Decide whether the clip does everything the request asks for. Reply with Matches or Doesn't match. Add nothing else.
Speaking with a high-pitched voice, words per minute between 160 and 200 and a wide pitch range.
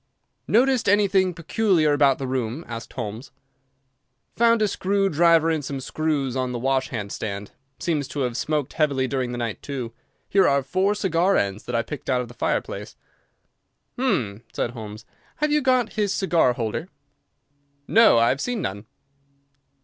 Doesn't match